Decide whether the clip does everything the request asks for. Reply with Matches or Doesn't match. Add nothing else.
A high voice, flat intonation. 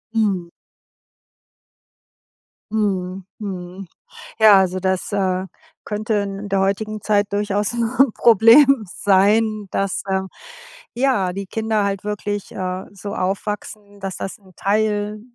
Matches